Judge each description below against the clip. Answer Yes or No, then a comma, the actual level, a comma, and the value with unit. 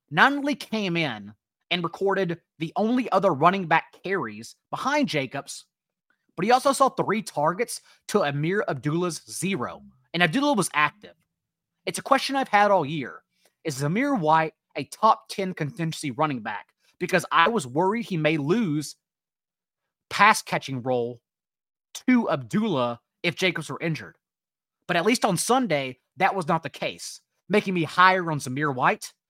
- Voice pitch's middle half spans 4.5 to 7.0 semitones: Yes, average, 5.2 semitones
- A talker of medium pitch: Yes, medium, 175 Hz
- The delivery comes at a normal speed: Yes, average, 155 wpm